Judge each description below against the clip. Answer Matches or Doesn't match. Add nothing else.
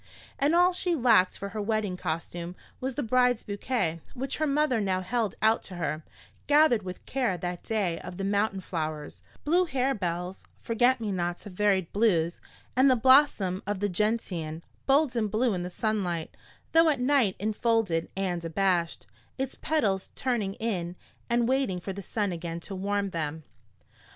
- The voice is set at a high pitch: Matches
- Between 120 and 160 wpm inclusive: Doesn't match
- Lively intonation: Matches